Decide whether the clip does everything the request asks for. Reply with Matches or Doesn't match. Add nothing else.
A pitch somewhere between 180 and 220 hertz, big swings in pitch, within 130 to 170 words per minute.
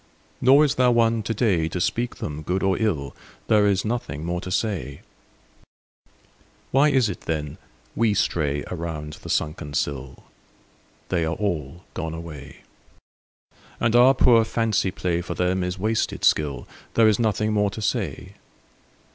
Doesn't match